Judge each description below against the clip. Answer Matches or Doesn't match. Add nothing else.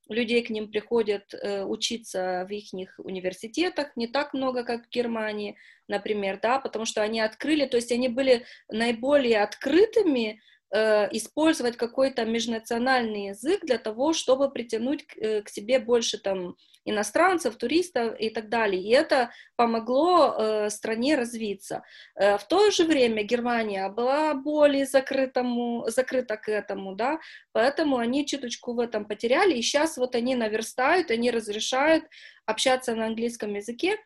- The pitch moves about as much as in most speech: Matches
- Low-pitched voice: Doesn't match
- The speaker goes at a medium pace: Matches